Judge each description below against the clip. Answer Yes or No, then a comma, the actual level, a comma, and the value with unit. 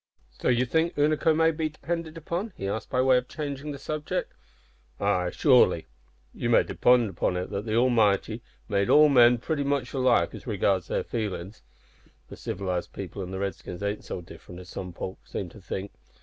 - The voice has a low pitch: Yes, low, 115 Hz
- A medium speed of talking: Yes, average, 190 wpm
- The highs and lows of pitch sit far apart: Yes, wide, 6.6 semitones